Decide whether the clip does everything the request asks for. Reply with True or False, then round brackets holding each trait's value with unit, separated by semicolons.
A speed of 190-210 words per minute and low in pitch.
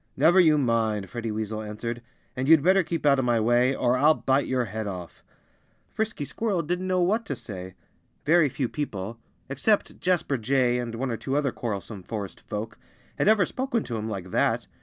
True (195 wpm; 125 Hz)